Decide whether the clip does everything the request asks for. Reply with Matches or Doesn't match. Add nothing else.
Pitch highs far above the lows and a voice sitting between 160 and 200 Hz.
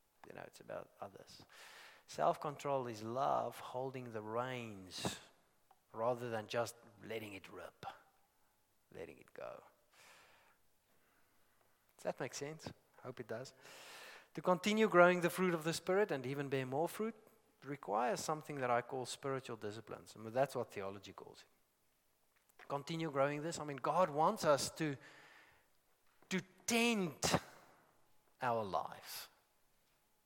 Doesn't match